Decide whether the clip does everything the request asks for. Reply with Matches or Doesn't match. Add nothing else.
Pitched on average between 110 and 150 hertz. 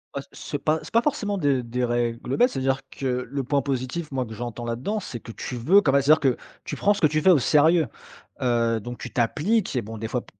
Matches